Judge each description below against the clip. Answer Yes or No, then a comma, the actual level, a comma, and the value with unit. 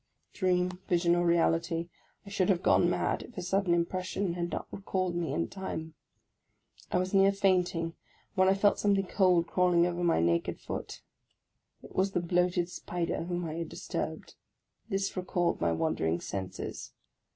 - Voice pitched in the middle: Yes, medium, 175 Hz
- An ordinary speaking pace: Yes, average, 165 wpm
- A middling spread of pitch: No, narrow, 1.9 semitones